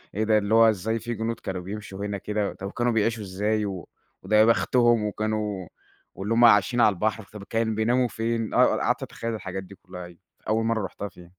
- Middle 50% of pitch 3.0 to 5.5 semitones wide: No, narrow, 2.4 semitones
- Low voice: Yes, low, 105 Hz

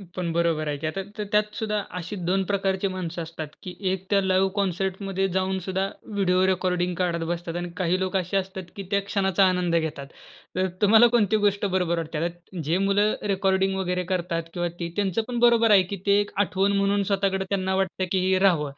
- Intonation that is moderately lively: No, narrow, 2.1 semitones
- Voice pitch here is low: No, high, 190 Hz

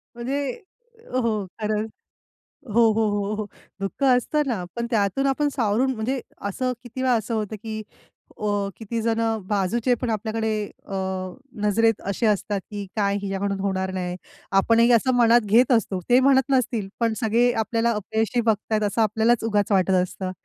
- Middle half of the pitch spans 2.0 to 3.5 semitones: Yes, average, 2.8 semitones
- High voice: Yes, high, 220 Hz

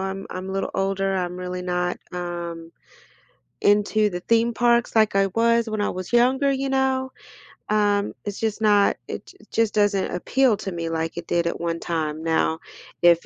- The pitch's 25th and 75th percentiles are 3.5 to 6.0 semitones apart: Yes, average, 4.2 semitones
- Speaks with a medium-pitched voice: No, high, 195 Hz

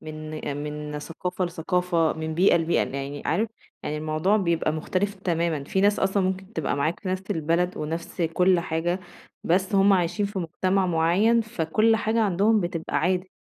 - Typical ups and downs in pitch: Yes, average, 3.1 semitones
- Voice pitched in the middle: Yes, medium, 175 Hz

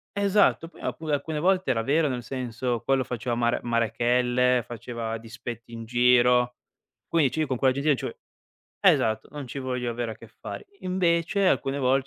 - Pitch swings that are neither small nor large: Yes, average, 3.4 semitones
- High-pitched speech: No, low, 125 Hz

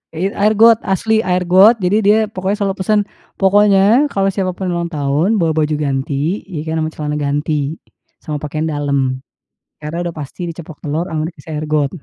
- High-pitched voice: No, medium, 170 Hz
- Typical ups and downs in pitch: Yes, average, 4.4 semitones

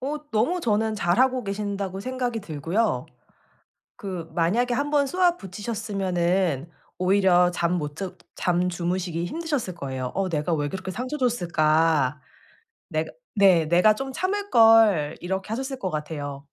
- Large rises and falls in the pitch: Yes, wide, 5.7 semitones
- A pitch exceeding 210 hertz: No, high, 190 Hz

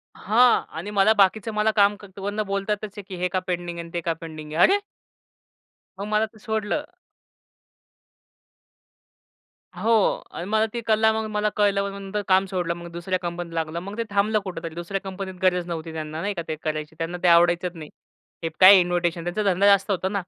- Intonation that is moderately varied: Yes, average, 3.2 semitones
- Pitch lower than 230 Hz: Yes, high, 190 Hz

